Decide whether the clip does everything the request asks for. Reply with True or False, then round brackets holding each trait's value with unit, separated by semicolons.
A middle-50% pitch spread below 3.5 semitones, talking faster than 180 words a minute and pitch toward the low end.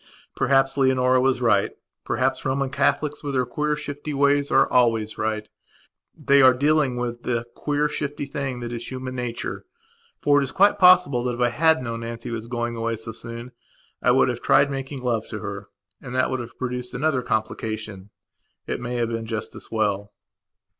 True (3.1 semitones; 190 wpm; 125 Hz)